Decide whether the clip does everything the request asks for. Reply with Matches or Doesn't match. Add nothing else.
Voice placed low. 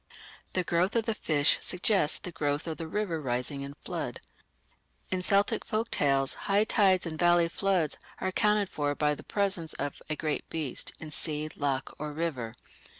Doesn't match